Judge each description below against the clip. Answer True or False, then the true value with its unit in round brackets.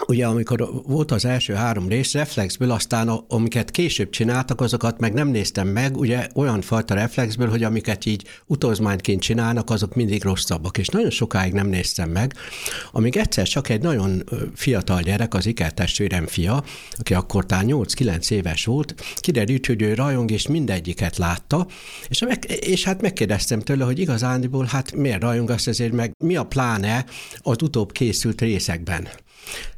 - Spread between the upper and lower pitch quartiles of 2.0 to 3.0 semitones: False (4.2 semitones)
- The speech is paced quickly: True (160 wpm)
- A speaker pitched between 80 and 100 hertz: False (115 Hz)